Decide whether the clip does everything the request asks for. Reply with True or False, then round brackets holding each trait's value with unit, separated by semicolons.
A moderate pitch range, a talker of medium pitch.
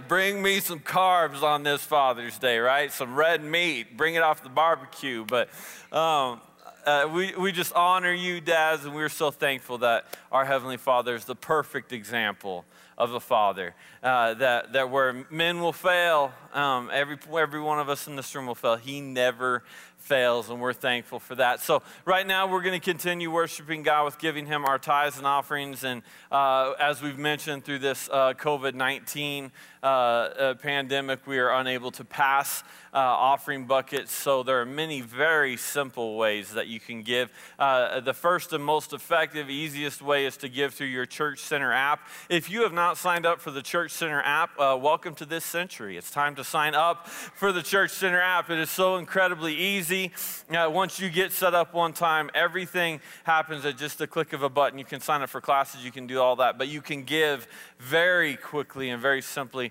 True (3.8 semitones; 145 Hz)